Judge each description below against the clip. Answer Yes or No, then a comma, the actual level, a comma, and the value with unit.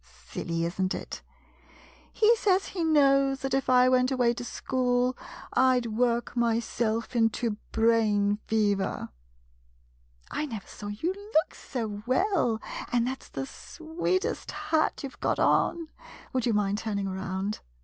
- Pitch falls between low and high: No, high, 240 Hz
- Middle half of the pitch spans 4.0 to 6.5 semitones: Yes, average, 4.5 semitones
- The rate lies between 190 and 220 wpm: No, average, 155 wpm